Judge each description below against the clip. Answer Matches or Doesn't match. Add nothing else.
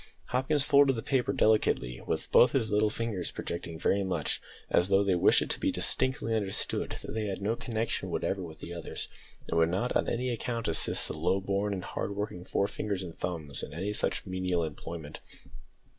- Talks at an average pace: Matches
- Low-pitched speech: Matches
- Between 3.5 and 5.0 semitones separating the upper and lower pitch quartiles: Matches